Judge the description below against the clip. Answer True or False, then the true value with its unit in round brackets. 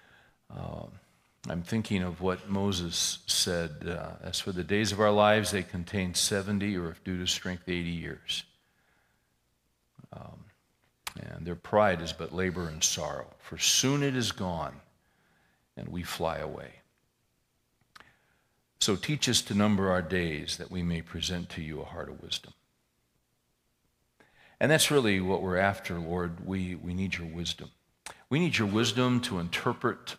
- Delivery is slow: False (155 wpm)